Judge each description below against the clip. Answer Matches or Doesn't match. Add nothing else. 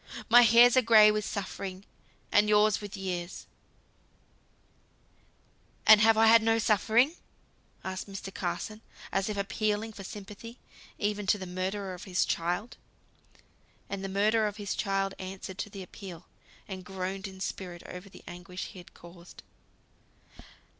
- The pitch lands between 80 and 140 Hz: Doesn't match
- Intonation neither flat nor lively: Doesn't match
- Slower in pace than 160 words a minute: Matches